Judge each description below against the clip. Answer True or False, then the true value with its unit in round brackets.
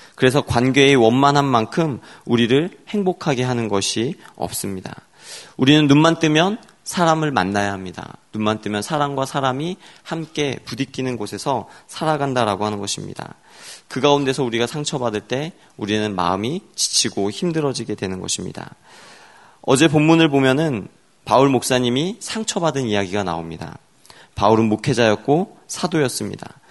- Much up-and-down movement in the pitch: True (6.1 semitones)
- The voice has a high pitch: False (130 Hz)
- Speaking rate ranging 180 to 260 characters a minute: False (330 characters per minute)